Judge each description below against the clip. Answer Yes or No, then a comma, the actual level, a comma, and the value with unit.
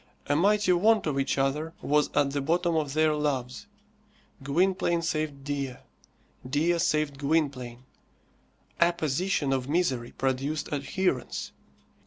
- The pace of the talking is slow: Yes, slow, 120 wpm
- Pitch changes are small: No, average, 3.7 semitones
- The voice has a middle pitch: Yes, medium, 150 Hz